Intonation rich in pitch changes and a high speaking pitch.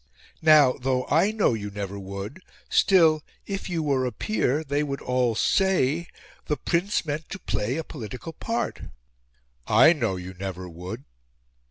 No: wide, 7.7 semitones; medium, 140 Hz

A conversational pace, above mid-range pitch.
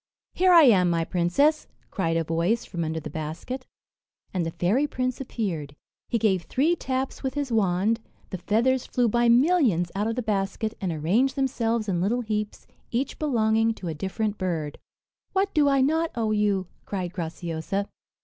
Yes: average, 175 wpm; high, 215 Hz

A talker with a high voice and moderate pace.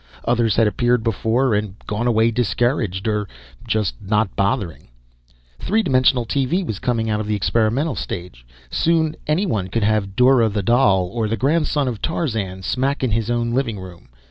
No: low, 115 Hz; average, 170 wpm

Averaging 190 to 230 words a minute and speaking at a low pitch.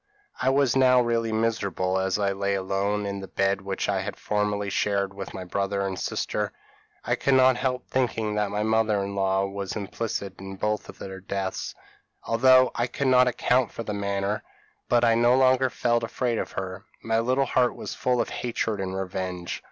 Yes: average, 195 wpm; low, 105 Hz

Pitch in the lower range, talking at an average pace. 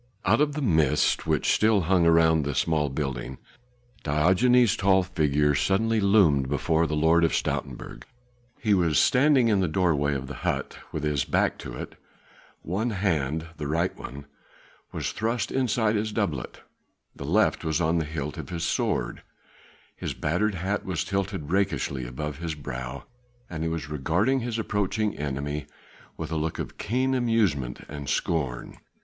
Yes: very low, 80 Hz; average, 165 wpm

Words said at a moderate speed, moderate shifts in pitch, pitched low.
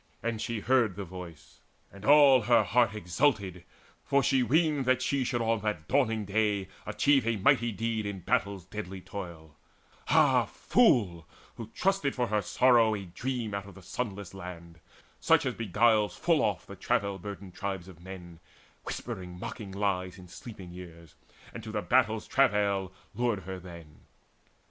Yes: average, 165 wpm; average, 4.4 semitones; low, 100 Hz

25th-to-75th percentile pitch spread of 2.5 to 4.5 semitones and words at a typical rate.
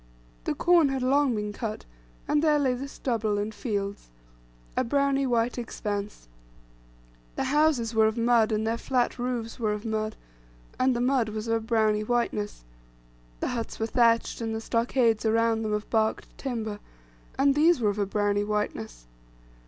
Yes: average, 2.9 semitones; average, 170 wpm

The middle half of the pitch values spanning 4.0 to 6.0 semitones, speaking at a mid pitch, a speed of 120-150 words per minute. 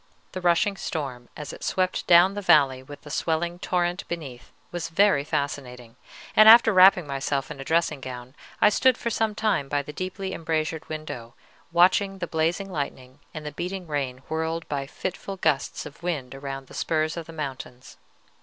No: average, 4.7 semitones; medium, 160 Hz; average, 180 wpm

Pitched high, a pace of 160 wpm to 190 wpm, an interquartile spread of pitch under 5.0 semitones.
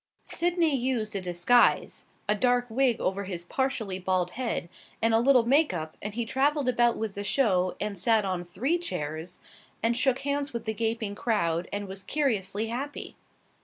No: high, 225 Hz; average, 175 wpm; average, 5.3 semitones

